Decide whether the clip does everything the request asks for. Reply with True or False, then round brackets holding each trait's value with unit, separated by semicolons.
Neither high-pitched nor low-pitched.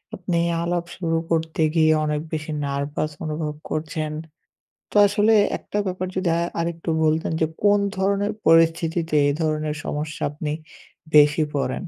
True (160 Hz)